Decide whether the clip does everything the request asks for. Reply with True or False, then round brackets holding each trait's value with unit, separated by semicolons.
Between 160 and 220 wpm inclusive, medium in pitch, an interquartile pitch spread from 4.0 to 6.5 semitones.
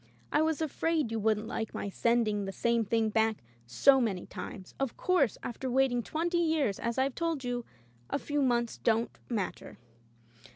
False (175 wpm; 235 Hz; 4.3 semitones)